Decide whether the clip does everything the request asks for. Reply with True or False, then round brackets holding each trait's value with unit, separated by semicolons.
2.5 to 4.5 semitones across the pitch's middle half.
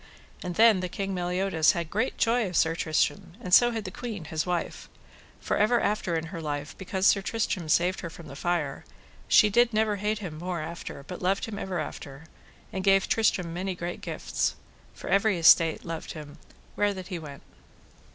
True (3.8 semitones)